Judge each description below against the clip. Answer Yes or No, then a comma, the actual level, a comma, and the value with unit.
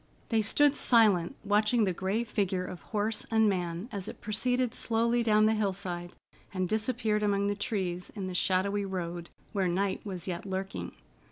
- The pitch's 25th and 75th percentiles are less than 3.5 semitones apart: Yes, average, 2.9 semitones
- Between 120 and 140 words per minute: No, average, 170 wpm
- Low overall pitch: No, high, 200 Hz